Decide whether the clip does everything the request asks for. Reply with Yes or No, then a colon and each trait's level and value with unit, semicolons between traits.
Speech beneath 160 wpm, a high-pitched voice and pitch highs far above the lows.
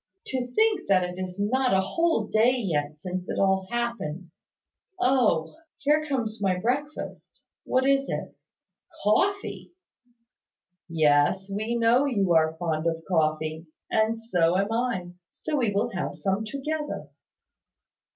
Yes: slow, 135 wpm; high, 205 Hz; wide, 6.3 semitones